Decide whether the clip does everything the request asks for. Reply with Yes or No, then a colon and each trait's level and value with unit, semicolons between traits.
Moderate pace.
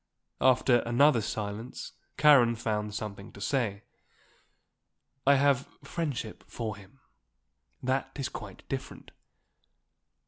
No: slow, 100 wpm